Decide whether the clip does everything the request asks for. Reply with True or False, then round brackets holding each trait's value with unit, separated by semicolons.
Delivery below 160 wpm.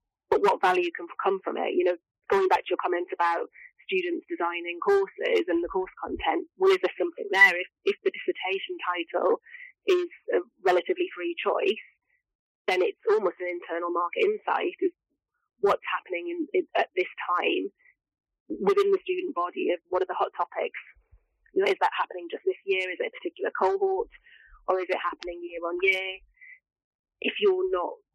False (180 wpm)